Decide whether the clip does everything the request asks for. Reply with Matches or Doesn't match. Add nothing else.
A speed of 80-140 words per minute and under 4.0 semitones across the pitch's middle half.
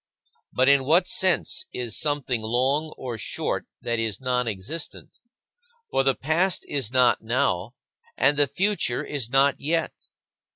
Matches